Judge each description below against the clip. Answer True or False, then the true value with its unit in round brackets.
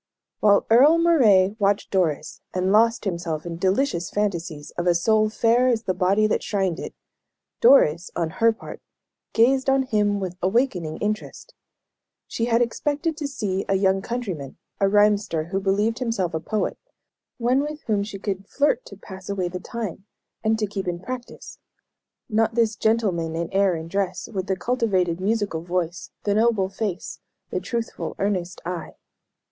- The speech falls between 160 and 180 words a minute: True (165 wpm)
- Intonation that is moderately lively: True (4.0 semitones)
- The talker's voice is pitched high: True (200 Hz)